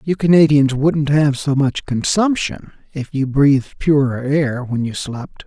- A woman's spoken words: No, male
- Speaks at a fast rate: No, average, 165 wpm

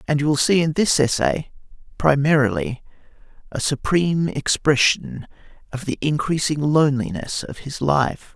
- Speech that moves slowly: Yes, slow, 130 wpm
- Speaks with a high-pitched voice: No, medium, 140 Hz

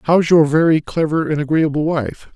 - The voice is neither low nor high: Yes, medium, 155 Hz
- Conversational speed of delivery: Yes, average, 180 wpm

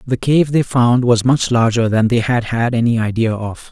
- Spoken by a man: Yes, male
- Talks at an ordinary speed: No, fast, 225 wpm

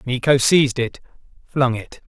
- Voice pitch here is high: No, low, 130 Hz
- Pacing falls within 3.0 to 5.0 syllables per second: Yes, 4.7 syllables/s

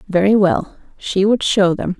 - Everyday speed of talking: Yes, average, 180 wpm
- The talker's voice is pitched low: No, high, 195 Hz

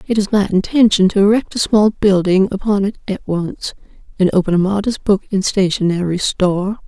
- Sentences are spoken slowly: No, average, 185 wpm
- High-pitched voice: Yes, high, 195 Hz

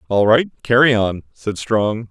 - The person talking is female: No, male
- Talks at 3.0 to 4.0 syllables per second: Yes, 3.9 syllables/s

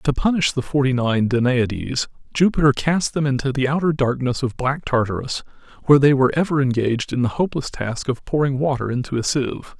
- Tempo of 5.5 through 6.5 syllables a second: Yes, 6.0 syllables/s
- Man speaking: Yes, male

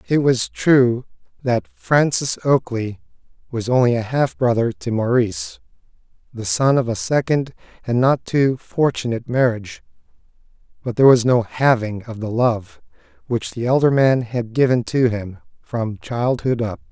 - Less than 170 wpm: Yes, average, 150 wpm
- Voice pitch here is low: Yes, low, 120 Hz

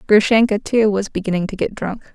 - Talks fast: No, average, 195 wpm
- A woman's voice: Yes, female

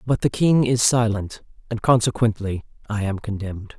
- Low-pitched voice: Yes, low, 110 Hz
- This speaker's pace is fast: No, average, 160 wpm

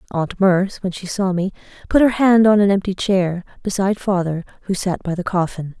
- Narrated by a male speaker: No, female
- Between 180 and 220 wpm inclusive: Yes, fast, 205 wpm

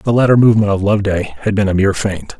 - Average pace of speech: No, fast, 250 wpm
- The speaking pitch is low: Yes, low, 100 Hz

